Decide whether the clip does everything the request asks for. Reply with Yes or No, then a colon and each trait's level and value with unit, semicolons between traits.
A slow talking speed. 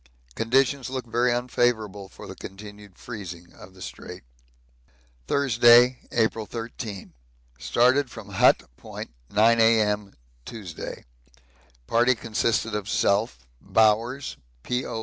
Yes: slow, 110 wpm